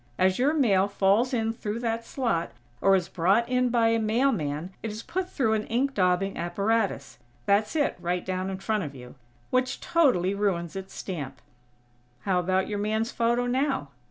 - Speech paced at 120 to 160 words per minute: No, average, 180 wpm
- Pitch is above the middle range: Yes, high, 210 Hz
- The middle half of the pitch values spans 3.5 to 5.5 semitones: Yes, average, 4.2 semitones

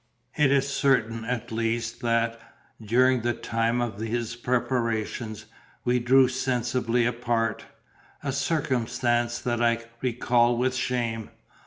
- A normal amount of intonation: No, narrow, 1.7 semitones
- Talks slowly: Yes, slow, 120 wpm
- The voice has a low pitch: Yes, low, 120 Hz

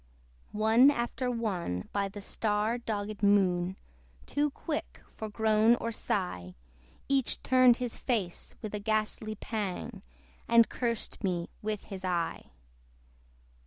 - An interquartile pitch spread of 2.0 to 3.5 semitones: Yes, average, 3.2 semitones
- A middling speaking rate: No, slow, 125 wpm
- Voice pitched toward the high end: Yes, high, 215 Hz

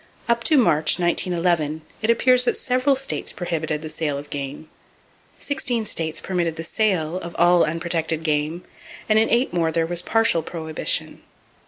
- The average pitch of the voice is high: No, medium, 170 Hz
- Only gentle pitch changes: No, wide, 5.6 semitones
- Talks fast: No, average, 160 wpm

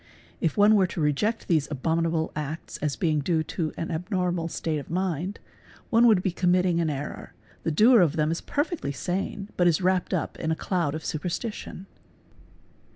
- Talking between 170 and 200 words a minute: Yes, average, 185 wpm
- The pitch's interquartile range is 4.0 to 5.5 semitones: No, average, 3.1 semitones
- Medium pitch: Yes, medium, 170 Hz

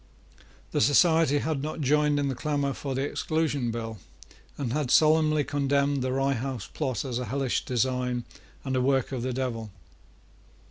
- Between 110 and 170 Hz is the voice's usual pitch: Yes, low, 135 Hz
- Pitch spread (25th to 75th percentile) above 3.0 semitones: No, narrow, 2.5 semitones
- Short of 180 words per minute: Yes, average, 170 wpm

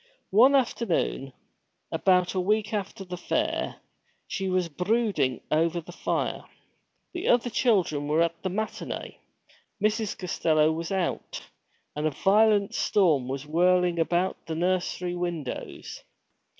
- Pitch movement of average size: Yes, average, 4.1 semitones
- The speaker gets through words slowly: Yes, slow, 125 wpm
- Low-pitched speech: No, medium, 180 Hz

